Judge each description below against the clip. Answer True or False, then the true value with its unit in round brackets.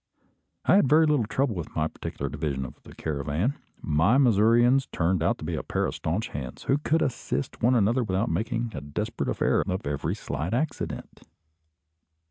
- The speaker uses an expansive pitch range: True (8.3 semitones)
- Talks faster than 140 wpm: True (180 wpm)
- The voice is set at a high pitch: False (95 Hz)